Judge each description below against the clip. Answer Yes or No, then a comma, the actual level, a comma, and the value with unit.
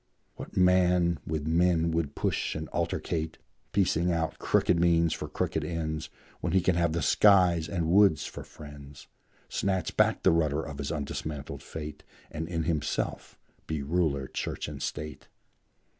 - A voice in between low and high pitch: No, very low, 80 Hz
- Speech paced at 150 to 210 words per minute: Yes, average, 155 wpm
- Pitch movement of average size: No, narrow, 2.2 semitones